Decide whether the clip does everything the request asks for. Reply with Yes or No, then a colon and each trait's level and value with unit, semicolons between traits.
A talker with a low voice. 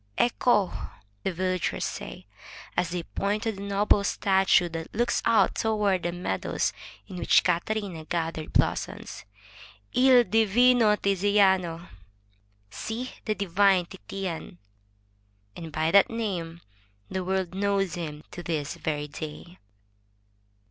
No: medium, 185 Hz